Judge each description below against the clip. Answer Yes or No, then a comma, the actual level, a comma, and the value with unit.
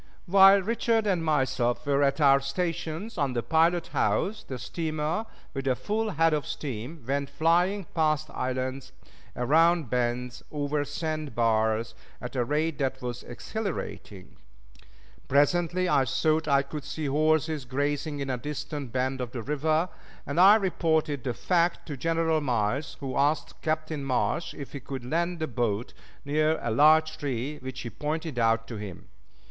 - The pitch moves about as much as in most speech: Yes, average, 3.9 semitones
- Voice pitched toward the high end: No, medium, 145 Hz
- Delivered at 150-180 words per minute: Yes, average, 160 wpm